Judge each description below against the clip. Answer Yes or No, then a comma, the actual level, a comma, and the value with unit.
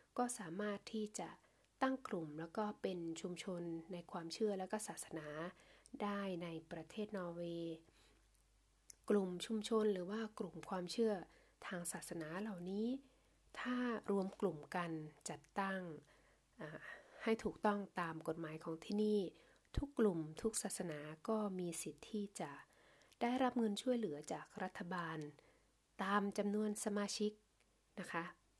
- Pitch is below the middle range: No, high, 195 Hz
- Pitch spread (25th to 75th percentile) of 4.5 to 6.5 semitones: No, average, 4.0 semitones